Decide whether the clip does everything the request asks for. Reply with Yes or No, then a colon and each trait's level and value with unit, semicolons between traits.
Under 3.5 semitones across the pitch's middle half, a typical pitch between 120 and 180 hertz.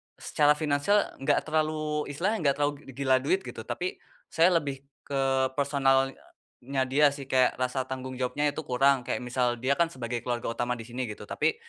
Yes: narrow, 2.6 semitones; low, 135 Hz